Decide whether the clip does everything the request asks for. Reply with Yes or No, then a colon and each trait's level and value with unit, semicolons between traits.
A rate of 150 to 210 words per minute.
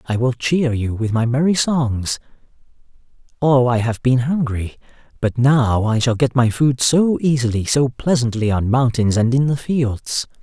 Yes: average, 175 wpm